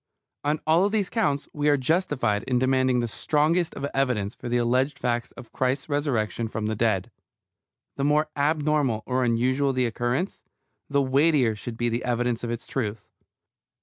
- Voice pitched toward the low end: Yes, low, 130 Hz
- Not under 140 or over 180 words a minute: Yes, average, 170 wpm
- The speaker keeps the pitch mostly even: No, average, 3.7 semitones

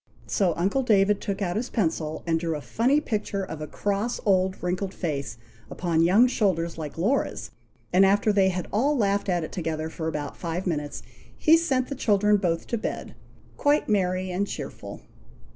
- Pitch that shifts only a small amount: No, average, 4.1 semitones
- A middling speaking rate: Yes, average, 180 wpm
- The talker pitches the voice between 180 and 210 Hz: Yes, high, 190 Hz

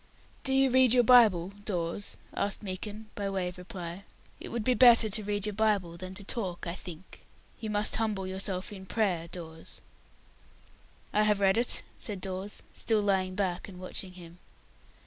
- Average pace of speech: Yes, average, 175 wpm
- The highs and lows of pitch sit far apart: No, average, 2.8 semitones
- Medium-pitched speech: No, high, 195 Hz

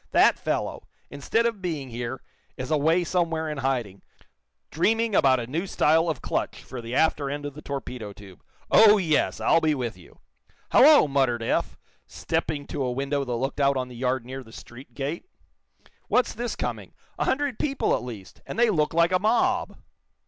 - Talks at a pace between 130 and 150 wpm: No, average, 185 wpm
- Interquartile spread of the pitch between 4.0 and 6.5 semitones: Yes, average, 5.3 semitones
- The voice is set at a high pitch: No, medium, 145 Hz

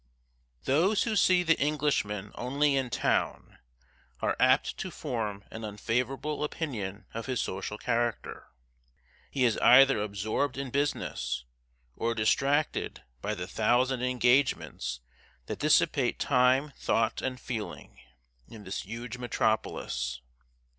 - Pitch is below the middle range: Yes, low, 125 Hz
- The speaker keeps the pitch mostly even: No, average, 4.3 semitones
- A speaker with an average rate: No, slow, 120 wpm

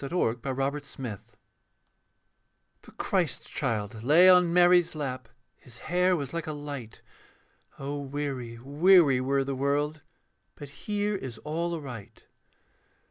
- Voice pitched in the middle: Yes, medium, 145 Hz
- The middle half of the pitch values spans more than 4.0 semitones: Yes, average, 4.5 semitones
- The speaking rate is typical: No, slow, 125 wpm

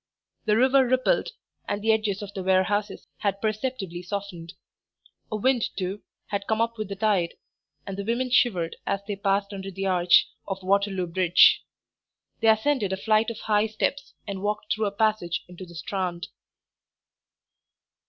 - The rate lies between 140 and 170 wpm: Yes, average, 165 wpm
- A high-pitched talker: Yes, high, 200 Hz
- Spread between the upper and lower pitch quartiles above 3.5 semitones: No, narrow, 2.5 semitones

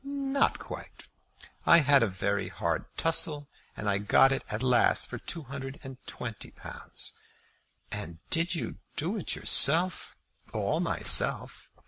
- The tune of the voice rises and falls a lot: Yes, wide, 7.0 semitones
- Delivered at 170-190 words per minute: No, slow, 135 wpm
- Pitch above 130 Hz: Yes, medium, 140 Hz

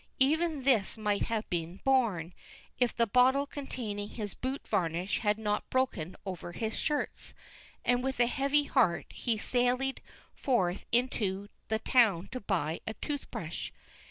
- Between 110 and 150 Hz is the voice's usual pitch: No, high, 230 Hz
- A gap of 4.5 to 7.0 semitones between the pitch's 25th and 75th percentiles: Yes, average, 4.8 semitones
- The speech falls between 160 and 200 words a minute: No, average, 150 wpm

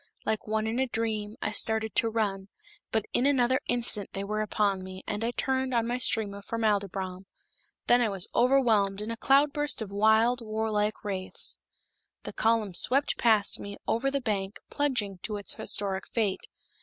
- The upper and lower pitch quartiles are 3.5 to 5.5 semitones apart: No, average, 3.0 semitones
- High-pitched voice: Yes, high, 220 Hz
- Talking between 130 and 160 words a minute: No, average, 180 wpm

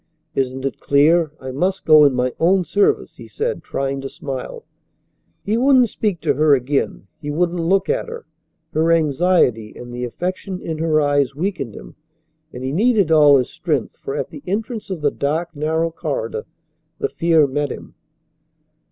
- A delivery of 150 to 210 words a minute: Yes, average, 175 wpm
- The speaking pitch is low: No, medium, 160 Hz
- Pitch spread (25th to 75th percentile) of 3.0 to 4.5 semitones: No, average, 5.3 semitones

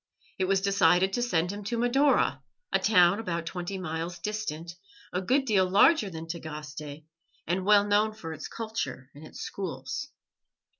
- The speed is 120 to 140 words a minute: No, average, 160 wpm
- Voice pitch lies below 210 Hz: Yes, medium, 185 Hz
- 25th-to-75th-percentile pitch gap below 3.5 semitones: No, average, 4.3 semitones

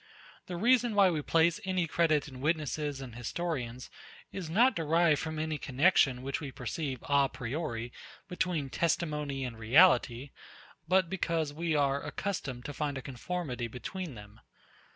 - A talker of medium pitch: Yes, medium, 150 Hz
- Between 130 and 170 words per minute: Yes, average, 150 wpm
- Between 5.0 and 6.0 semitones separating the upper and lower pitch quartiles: No, average, 4.4 semitones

